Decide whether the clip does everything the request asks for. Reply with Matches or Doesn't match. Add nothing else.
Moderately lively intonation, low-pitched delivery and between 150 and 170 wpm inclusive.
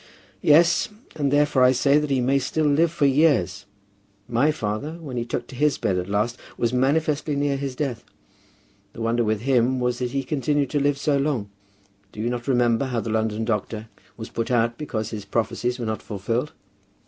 Doesn't match